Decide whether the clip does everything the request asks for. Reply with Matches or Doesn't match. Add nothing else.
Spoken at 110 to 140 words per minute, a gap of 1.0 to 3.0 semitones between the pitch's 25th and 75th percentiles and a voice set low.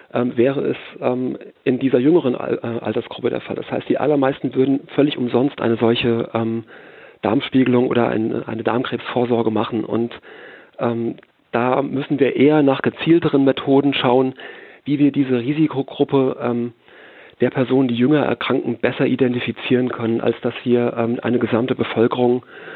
Matches